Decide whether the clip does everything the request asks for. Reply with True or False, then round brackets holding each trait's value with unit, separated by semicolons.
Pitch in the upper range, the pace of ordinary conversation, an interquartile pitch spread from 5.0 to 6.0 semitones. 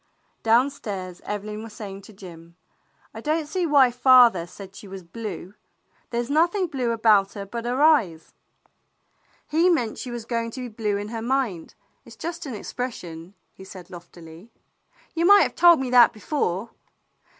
True (230 Hz; 170 wpm; 5.5 semitones)